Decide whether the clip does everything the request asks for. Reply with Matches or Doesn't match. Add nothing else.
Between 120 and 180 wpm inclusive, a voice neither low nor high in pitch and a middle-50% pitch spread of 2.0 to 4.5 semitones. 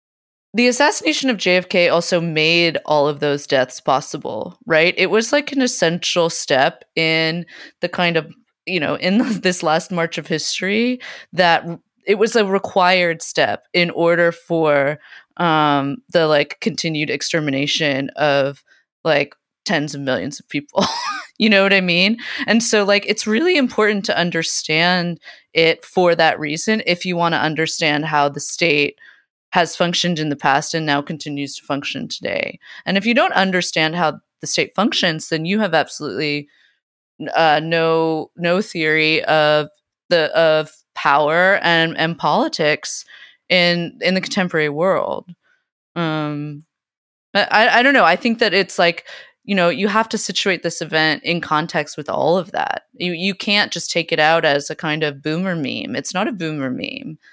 Matches